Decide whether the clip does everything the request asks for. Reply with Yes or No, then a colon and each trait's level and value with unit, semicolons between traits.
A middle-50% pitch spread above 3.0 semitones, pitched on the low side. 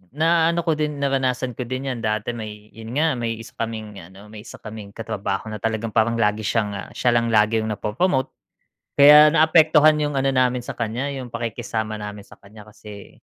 Yes: average, 4.2 semitones; low, 115 Hz